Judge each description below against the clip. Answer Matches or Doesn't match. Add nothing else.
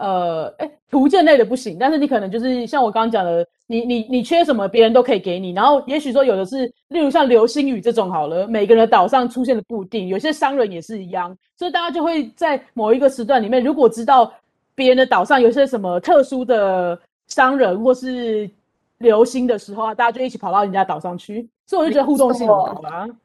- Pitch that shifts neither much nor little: Matches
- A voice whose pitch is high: Matches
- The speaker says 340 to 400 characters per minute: Matches